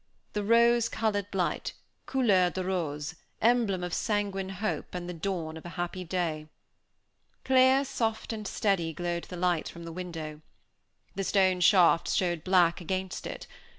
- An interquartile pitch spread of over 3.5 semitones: No, average, 3.1 semitones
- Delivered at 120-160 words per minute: Yes, average, 150 wpm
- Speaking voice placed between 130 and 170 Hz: No, medium, 185 Hz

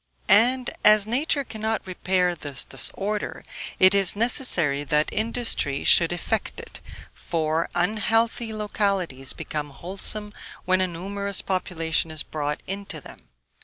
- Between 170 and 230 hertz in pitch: Yes, medium, 185 Hz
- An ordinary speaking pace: No, slow, 125 wpm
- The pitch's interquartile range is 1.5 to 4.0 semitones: No, average, 4.7 semitones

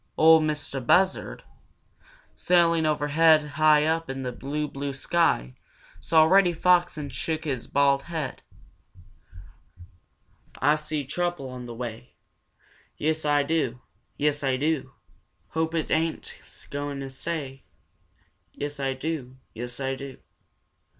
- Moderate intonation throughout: Yes, average, 3.0 semitones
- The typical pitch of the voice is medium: Yes, medium, 150 Hz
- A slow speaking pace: Yes, slow, 130 wpm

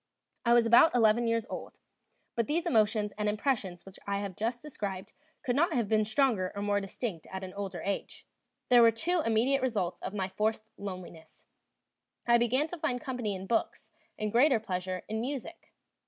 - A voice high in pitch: Yes, high, 220 Hz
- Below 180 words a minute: No, average, 185 wpm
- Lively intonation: No, average, 3.7 semitones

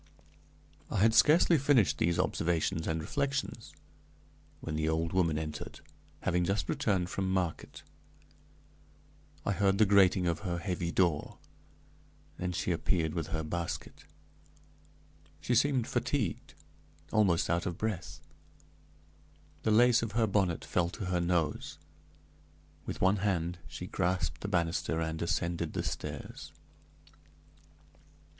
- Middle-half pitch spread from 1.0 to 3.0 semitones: No, average, 3.7 semitones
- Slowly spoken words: Yes, slow, 125 wpm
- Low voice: Yes, very low, 90 Hz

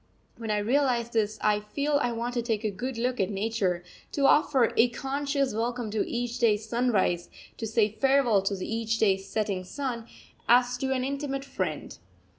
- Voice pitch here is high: Yes, high, 235 Hz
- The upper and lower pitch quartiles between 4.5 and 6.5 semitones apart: No, average, 3.4 semitones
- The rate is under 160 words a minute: No, average, 180 wpm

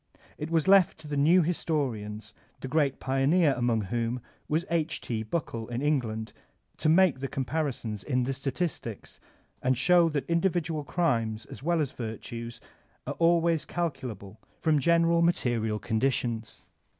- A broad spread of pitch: Yes, wide, 6.0 semitones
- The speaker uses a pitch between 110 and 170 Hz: Yes, medium, 140 Hz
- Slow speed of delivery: No, average, 150 wpm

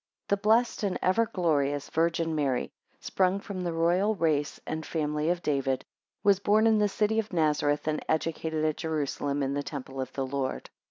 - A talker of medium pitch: Yes, medium, 160 Hz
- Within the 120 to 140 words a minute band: No, average, 180 wpm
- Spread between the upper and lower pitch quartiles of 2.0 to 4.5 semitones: No, average, 4.9 semitones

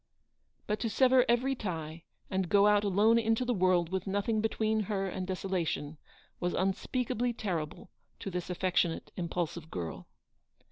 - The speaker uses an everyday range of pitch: Yes, average, 3.8 semitones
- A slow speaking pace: No, average, 150 wpm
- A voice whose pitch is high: Yes, high, 195 Hz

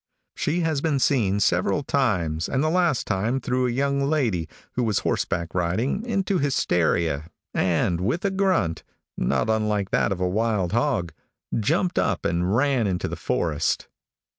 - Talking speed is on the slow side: No, average, 160 wpm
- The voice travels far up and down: Yes, wide, 7.8 semitones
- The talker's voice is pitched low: Yes, low, 110 Hz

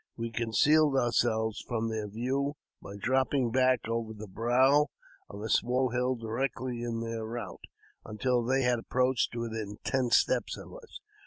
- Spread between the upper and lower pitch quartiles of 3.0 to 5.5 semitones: No, narrow, 2.5 semitones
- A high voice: No, low, 120 Hz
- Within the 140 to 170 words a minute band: Yes, average, 155 wpm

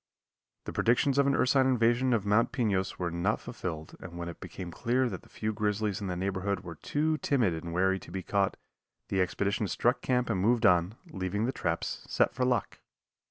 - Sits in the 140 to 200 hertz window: No, low, 100 Hz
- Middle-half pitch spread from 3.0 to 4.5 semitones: No, average, 4.9 semitones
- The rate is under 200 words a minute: No, fast, 205 wpm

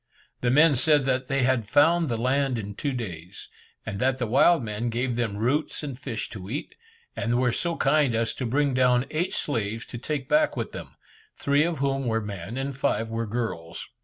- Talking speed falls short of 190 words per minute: No, fast, 205 wpm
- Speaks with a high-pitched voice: No, low, 125 Hz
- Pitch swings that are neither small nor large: Yes, average, 3.8 semitones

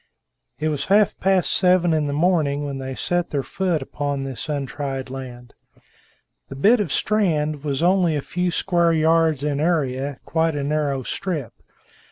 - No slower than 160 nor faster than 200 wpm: Yes, average, 165 wpm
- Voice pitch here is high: No, medium, 150 Hz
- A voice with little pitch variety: No, average, 4.0 semitones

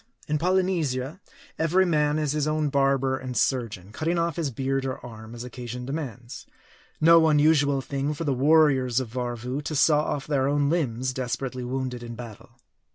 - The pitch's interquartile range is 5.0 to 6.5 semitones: No, average, 3.5 semitones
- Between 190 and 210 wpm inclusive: No, average, 170 wpm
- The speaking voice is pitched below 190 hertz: Yes, low, 135 Hz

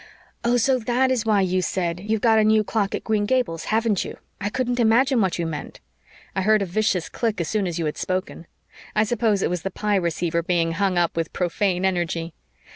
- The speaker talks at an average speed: No, fast, 220 wpm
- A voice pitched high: Yes, high, 200 Hz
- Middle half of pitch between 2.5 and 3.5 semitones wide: No, average, 4.1 semitones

